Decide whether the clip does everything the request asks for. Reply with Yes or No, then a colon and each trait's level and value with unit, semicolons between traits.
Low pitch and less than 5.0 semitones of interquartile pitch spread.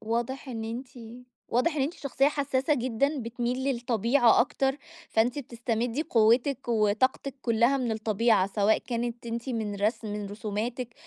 No: high, 235 Hz; average, 2.8 semitones